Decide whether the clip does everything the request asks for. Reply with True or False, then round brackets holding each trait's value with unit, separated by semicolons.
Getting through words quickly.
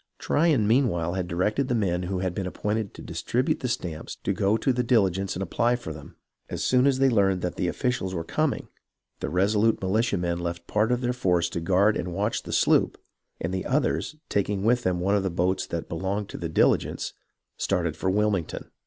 True (215 wpm)